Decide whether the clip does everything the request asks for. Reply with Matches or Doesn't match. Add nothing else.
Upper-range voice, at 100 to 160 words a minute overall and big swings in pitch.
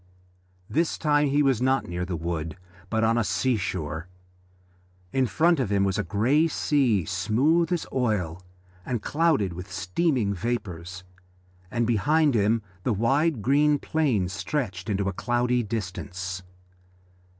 Doesn't match